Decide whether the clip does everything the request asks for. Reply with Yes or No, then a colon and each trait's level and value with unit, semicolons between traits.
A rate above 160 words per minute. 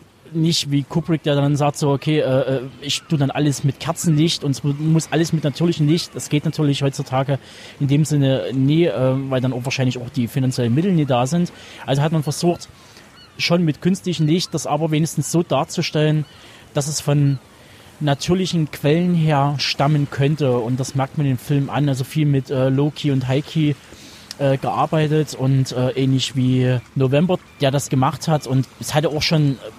Yes: average, 185 wpm